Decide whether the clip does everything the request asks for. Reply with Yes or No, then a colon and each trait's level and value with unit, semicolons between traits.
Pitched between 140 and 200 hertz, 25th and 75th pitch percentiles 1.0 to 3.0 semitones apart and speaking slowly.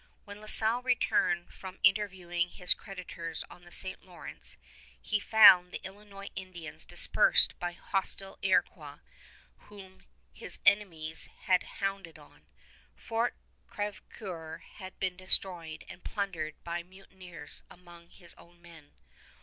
Yes: medium, 185 Hz; narrow, 2.4 semitones; slow, 125 wpm